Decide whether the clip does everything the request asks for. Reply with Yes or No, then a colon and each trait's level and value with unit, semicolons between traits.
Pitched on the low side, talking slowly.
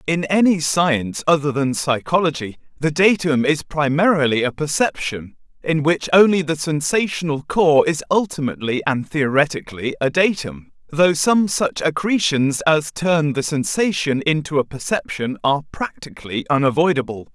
No: medium, 155 Hz; slow, 130 wpm